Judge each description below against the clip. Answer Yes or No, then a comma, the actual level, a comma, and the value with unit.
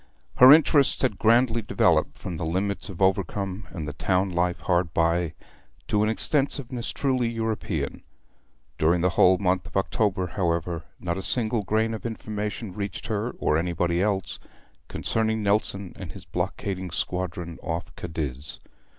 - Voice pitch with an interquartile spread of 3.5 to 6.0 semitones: Yes, average, 4.2 semitones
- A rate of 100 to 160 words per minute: Yes, average, 150 wpm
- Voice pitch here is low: Yes, very low, 95 Hz